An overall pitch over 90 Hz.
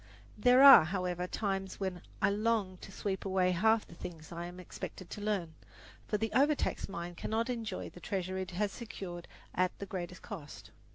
Yes: high, 190 Hz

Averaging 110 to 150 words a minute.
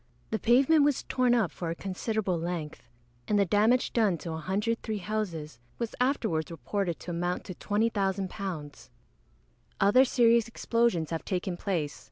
Yes: average, 145 wpm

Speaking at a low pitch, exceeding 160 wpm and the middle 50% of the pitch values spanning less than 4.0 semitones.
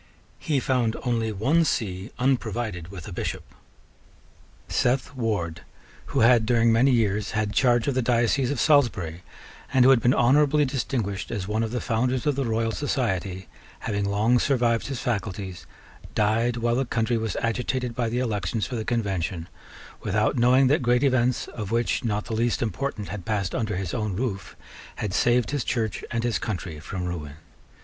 Yes: low, 115 Hz; average, 175 wpm; average, 3.4 semitones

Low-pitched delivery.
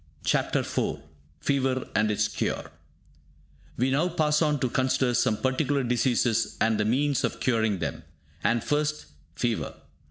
Yes: low, 130 Hz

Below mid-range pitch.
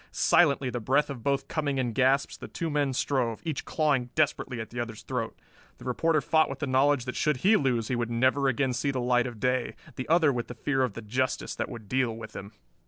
Yes: low, 130 Hz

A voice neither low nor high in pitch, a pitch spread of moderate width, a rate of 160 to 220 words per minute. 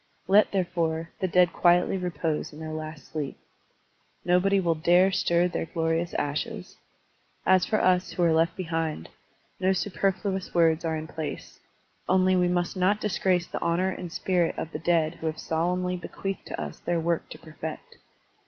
No: medium, 175 Hz; narrow, 2.3 semitones; average, 170 wpm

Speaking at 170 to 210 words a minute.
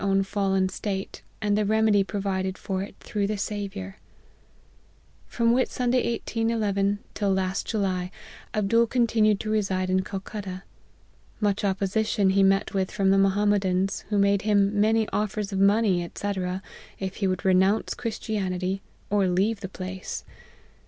No: average, 145 wpm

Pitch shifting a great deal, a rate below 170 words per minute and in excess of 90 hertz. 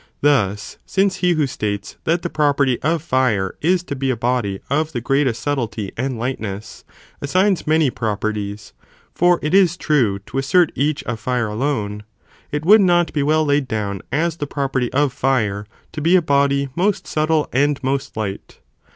No: wide, 5.7 semitones; average, 175 wpm; medium, 140 Hz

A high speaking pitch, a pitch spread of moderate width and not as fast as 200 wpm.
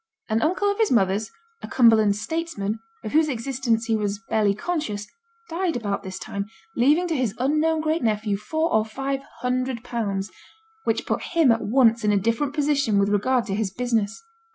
No: high, 230 Hz; wide, 5.8 semitones; average, 180 wpm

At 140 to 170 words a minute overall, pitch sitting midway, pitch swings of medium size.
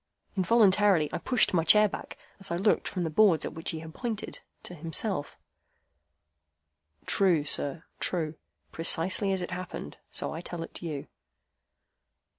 Yes: average, 145 wpm; medium, 175 Hz; average, 3.4 semitones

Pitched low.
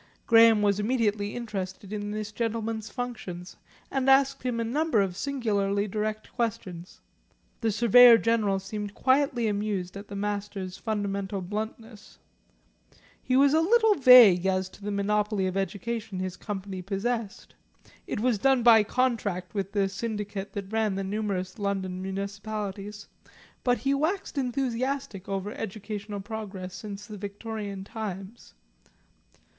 No: high, 210 Hz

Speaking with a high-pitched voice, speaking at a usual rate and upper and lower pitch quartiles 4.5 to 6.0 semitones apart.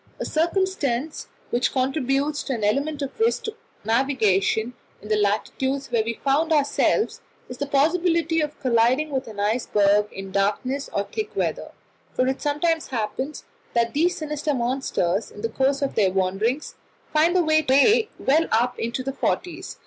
Yes: very high, 270 Hz; average, 155 wpm; average, 5.2 semitones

